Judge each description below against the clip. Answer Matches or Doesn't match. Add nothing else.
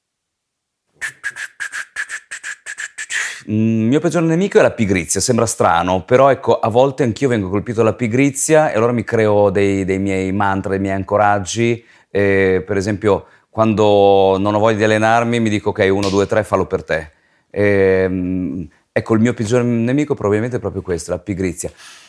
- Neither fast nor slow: Matches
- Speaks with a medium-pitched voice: Doesn't match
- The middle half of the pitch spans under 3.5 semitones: Doesn't match